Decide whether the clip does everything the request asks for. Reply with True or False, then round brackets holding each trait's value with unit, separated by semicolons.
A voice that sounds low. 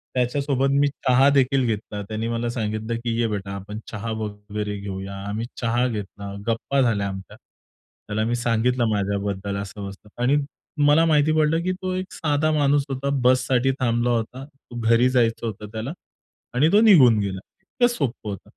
True (115 Hz)